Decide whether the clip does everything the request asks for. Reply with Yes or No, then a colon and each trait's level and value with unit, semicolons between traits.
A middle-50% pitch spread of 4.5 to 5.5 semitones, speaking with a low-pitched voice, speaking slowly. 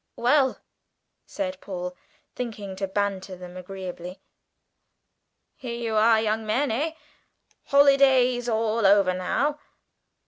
No: average, 4.9 semitones; high, 220 Hz; slow, 105 wpm